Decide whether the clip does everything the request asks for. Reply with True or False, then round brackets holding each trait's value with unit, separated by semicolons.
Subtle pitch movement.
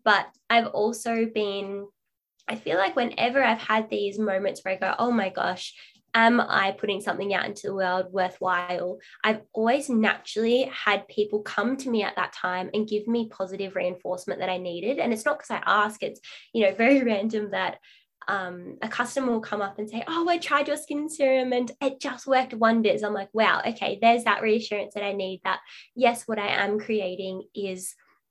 False (3.3 semitones)